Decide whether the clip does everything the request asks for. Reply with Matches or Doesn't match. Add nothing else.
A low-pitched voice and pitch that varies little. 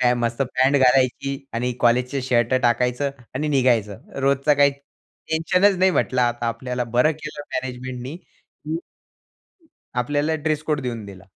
Doesn't match